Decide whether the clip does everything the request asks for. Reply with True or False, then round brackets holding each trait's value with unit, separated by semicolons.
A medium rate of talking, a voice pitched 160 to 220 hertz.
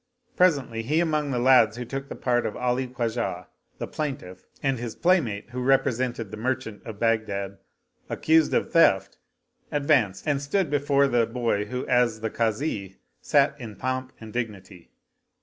False (165 wpm; 125 Hz)